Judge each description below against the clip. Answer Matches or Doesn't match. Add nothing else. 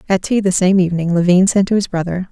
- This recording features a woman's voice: Matches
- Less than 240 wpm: Doesn't match